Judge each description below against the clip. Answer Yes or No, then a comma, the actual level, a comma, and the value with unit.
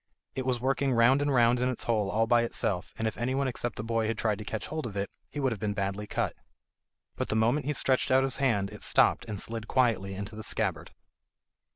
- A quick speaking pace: Yes, fast, 240 wpm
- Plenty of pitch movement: No, average, 3.6 semitones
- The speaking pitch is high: No, low, 115 Hz